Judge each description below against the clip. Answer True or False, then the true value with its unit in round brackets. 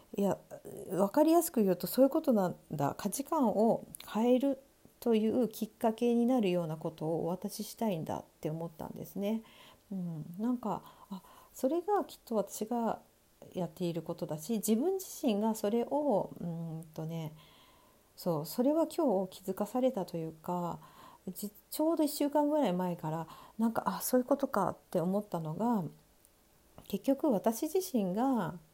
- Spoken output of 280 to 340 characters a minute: True (310 characters per minute)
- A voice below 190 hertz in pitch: False (210 Hz)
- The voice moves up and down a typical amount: False (6.5 semitones)